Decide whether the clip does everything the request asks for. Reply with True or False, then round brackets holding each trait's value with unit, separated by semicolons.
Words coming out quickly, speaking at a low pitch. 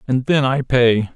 True (210 wpm; 125 Hz)